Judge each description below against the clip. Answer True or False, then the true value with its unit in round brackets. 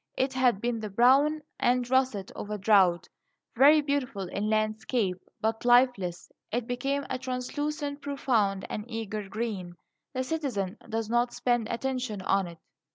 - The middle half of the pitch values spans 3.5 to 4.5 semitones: True (4.0 semitones)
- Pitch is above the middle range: True (240 Hz)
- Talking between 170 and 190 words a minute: False (145 wpm)